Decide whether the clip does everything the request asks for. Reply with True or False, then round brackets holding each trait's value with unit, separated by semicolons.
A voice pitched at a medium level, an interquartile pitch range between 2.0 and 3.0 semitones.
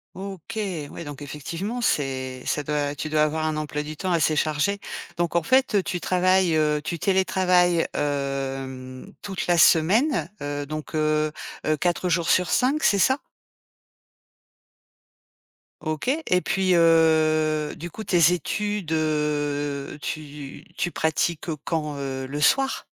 False (155 Hz; 3.6 semitones)